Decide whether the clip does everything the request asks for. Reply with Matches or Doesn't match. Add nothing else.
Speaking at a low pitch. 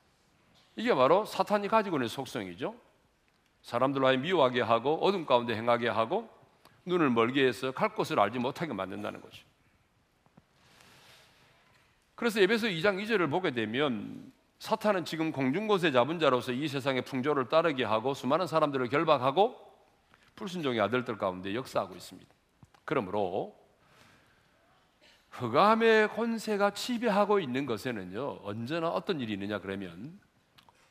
Doesn't match